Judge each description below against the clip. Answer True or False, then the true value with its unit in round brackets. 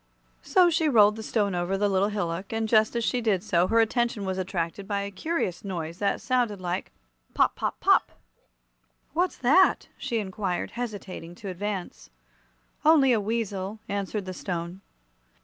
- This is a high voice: True (205 Hz)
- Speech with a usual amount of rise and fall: True (3.6 semitones)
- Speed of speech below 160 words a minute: False (165 wpm)